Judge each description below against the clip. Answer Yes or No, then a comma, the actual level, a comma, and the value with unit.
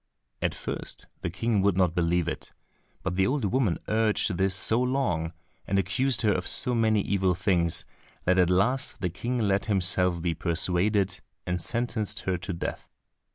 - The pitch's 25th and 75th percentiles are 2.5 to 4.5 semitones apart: Yes, average, 3.8 semitones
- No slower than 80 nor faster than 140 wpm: No, average, 170 wpm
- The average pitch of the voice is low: Yes, very low, 95 Hz